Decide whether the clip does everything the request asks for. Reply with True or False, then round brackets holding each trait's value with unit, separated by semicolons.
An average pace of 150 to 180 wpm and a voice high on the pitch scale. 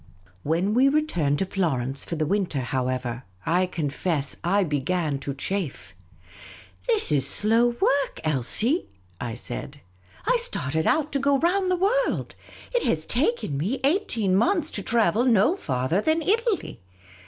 True (155 wpm; 195 Hz)